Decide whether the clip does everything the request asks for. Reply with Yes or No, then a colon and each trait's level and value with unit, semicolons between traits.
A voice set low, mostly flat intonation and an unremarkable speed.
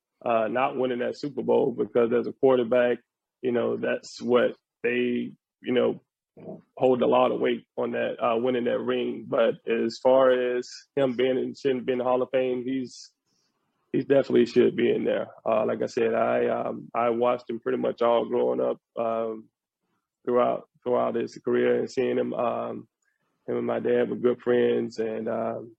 Yes: low, 120 Hz; narrow, 1.9 semitones; average, 185 wpm